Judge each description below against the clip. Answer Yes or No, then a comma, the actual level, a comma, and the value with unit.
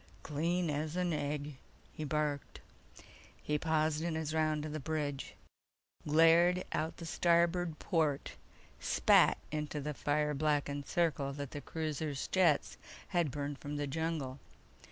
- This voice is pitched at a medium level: Yes, medium, 155 Hz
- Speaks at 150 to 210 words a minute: No, slow, 135 wpm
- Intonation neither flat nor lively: No, narrow, 2.0 semitones